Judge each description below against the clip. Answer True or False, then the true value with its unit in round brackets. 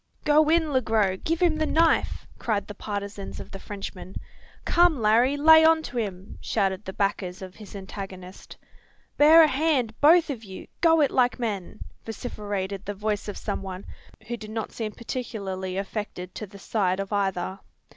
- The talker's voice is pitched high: True (210 Hz)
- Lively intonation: True (6.1 semitones)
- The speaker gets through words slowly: False (175 wpm)